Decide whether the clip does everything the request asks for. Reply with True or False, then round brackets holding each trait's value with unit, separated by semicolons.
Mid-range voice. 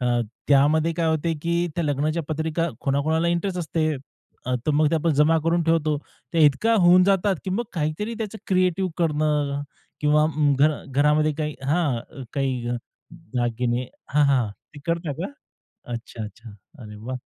True (155 Hz)